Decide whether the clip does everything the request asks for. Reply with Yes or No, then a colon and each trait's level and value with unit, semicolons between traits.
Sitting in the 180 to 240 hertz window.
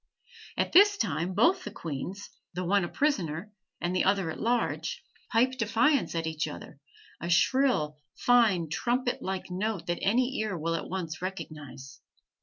Yes: high, 190 Hz